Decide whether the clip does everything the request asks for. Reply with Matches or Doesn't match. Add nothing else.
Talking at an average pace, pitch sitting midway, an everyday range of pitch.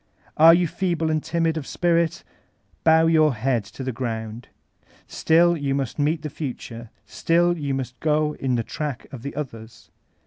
Matches